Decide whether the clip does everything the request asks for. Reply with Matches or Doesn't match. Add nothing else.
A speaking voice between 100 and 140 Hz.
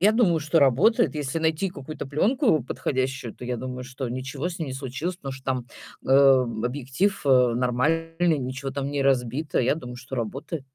Matches